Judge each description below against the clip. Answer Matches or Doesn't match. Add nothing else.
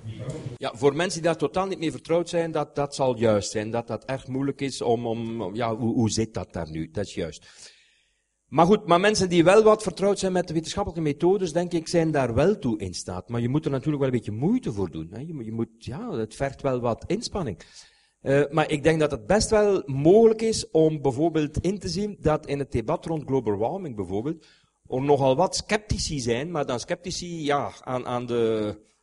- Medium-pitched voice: Matches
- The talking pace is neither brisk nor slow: Doesn't match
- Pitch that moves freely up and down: Matches